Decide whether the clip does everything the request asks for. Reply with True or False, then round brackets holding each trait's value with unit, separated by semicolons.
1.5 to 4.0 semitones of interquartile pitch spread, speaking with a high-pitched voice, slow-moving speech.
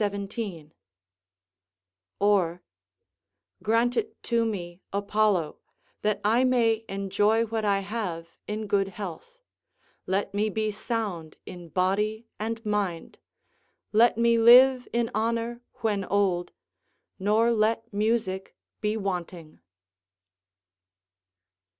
True (2.9 semitones; 210 Hz; 100 wpm)